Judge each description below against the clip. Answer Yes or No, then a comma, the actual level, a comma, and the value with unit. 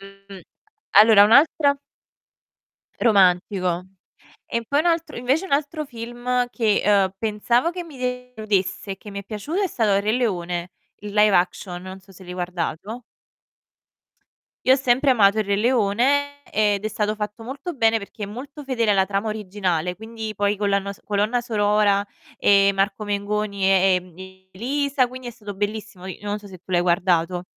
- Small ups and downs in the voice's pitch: No, average, 3.7 semitones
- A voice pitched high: Yes, high, 210 Hz